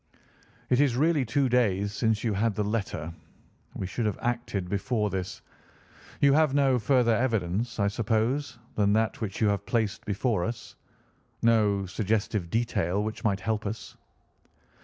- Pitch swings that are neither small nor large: Yes, average, 3.0 semitones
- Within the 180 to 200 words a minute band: No, average, 150 wpm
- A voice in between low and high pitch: No, low, 110 Hz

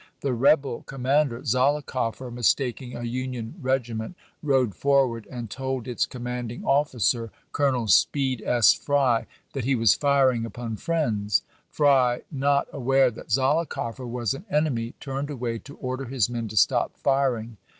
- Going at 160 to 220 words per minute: No, average, 150 wpm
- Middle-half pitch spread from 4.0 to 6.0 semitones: No, average, 2.8 semitones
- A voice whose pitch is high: No, low, 130 Hz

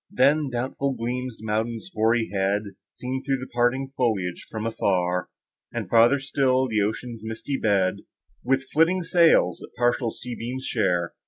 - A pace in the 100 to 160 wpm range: Yes, average, 150 wpm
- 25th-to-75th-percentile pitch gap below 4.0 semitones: Yes, average, 3.4 semitones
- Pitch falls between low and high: No, low, 120 Hz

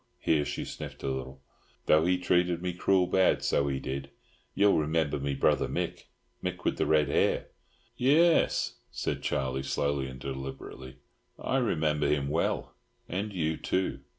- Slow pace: No, average, 150 wpm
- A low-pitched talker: Yes, very low, 75 Hz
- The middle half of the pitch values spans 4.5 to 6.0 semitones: Yes, average, 4.9 semitones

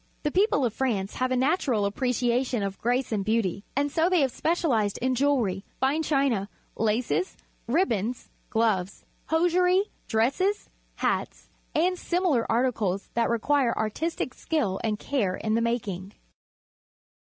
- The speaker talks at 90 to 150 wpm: Yes, average, 145 wpm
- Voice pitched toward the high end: Yes, high, 245 Hz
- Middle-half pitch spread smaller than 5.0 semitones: No, average, 5.3 semitones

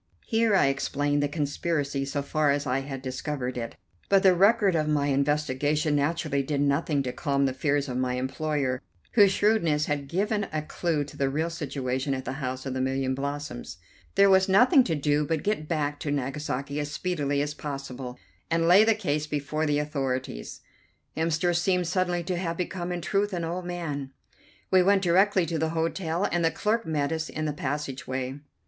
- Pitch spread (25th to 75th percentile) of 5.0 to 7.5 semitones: No, average, 3.8 semitones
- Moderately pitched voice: Yes, medium, 150 Hz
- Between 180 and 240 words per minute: Yes, average, 195 wpm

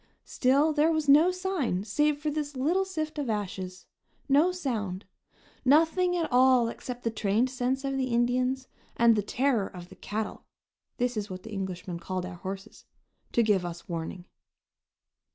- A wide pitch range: Yes, wide, 6.8 semitones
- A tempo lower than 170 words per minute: Yes, average, 160 wpm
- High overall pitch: Yes, high, 245 Hz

